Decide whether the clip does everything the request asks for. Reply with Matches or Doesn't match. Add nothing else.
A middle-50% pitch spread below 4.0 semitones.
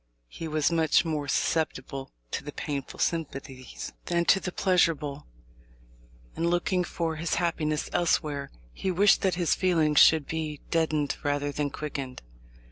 Matches